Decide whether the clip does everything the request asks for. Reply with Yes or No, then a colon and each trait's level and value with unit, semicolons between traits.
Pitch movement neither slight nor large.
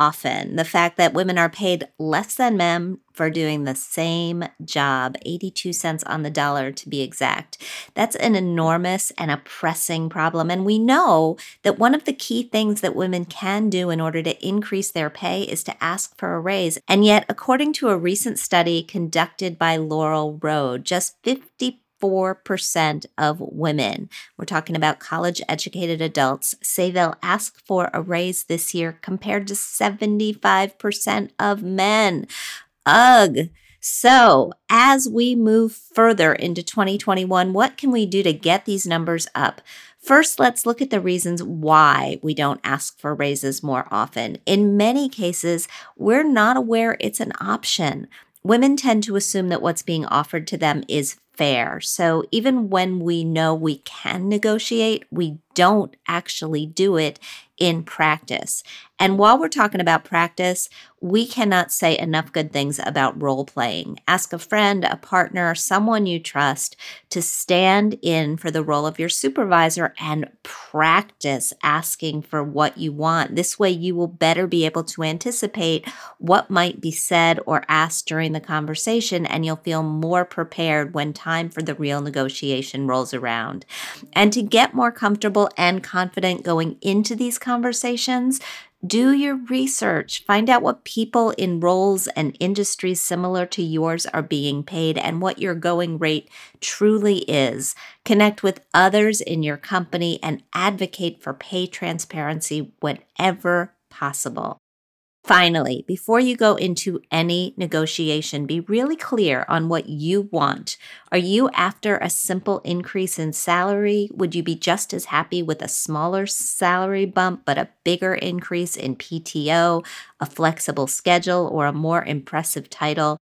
Yes: average, 4.1 semitones